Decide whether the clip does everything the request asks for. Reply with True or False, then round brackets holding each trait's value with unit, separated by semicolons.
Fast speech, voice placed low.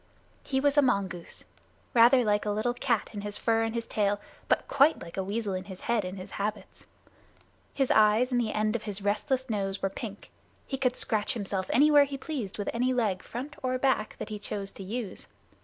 False (210 wpm; 215 Hz)